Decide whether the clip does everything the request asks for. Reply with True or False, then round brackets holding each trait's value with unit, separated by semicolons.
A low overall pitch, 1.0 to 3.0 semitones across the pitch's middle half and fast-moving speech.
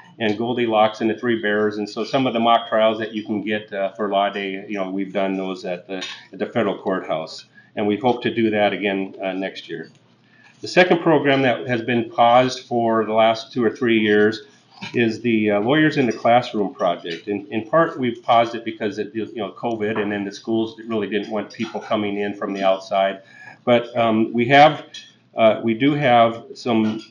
True (110 Hz; 2.5 semitones; 220 wpm)